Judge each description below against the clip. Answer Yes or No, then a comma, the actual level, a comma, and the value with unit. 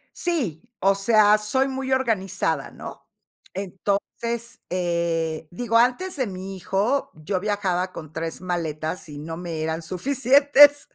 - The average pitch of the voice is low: No, high, 195 Hz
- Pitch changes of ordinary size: No, wide, 6.1 semitones